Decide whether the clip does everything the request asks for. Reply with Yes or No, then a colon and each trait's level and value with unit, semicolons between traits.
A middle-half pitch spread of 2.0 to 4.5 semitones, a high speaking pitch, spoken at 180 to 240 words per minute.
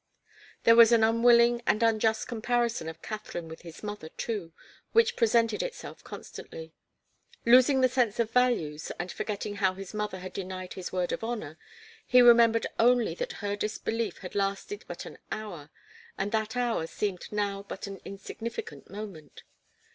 No: average, 3.4 semitones; high, 215 Hz; average, 160 wpm